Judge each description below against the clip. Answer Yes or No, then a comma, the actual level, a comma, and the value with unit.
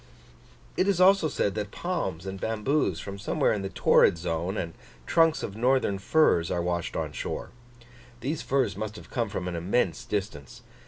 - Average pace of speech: Yes, average, 175 wpm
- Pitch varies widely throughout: Yes, wide, 7.0 semitones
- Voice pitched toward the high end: No, low, 100 Hz